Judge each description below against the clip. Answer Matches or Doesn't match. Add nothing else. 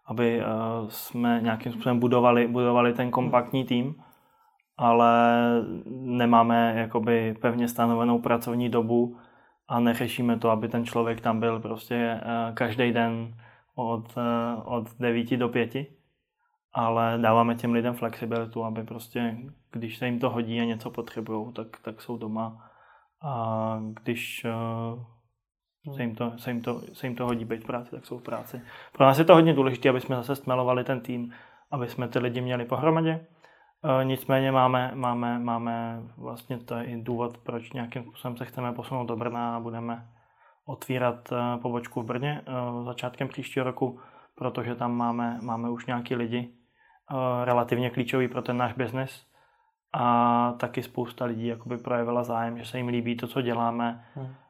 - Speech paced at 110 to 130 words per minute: Doesn't match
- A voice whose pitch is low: Matches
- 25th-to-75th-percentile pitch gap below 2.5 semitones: Matches